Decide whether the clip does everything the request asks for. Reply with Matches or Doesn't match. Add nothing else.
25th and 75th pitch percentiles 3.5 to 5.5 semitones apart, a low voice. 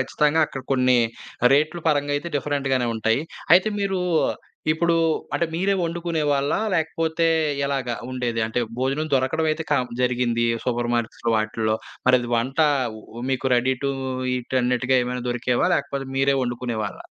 Matches